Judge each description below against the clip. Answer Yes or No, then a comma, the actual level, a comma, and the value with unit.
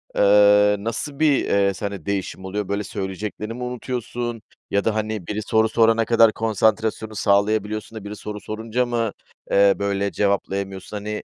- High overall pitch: No, low, 105 Hz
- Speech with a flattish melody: Yes, narrow, 1.9 semitones